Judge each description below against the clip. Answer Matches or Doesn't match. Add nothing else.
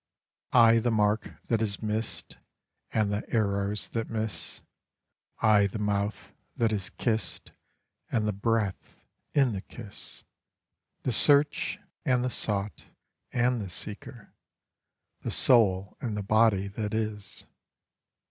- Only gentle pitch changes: Matches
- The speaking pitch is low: Matches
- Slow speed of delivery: Matches